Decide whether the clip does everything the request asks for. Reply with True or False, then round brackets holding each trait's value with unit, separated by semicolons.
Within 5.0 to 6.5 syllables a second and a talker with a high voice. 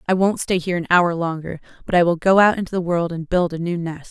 False (6.3 syllables/s; 175 Hz)